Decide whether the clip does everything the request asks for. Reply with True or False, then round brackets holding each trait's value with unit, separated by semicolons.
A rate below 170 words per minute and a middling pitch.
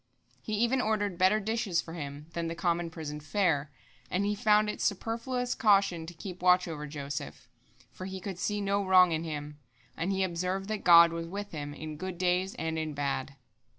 False (195 wpm; 180 Hz)